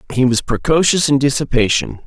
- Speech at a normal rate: Yes, average, 145 wpm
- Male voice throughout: Yes, male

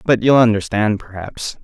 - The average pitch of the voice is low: Yes, low, 110 Hz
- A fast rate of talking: No, average, 145 wpm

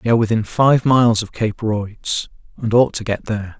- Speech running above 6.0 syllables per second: No, 5.4 syllables/s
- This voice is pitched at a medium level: No, low, 110 Hz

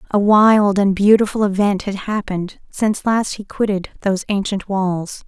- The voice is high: Yes, high, 200 Hz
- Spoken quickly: No, average, 160 wpm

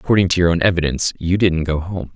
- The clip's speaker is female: No, male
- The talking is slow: No, fast, 250 wpm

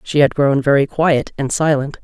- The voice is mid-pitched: Yes, medium, 145 Hz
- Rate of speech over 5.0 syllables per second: No, 4.9 syllables/s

